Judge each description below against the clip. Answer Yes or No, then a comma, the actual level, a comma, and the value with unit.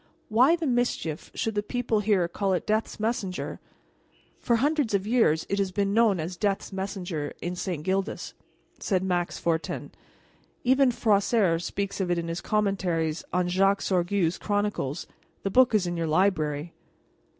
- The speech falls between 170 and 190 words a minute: No, average, 160 wpm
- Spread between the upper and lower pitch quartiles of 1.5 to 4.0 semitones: Yes, average, 3.6 semitones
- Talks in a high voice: Yes, high, 195 Hz